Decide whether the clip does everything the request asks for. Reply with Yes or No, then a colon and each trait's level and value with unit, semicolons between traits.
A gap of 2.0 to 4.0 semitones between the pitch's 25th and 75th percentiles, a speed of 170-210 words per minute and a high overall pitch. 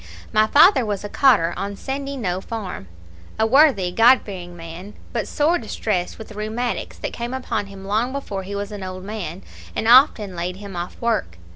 No: average, 4.4 semitones; average, 185 wpm; high, 210 Hz